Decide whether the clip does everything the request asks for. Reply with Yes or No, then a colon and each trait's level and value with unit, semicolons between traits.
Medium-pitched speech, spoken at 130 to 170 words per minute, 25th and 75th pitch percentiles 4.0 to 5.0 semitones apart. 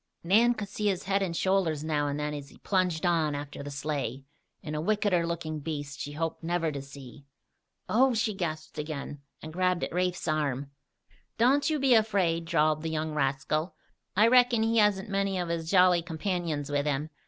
No: medium, 165 Hz; average, 190 wpm; average, 4.5 semitones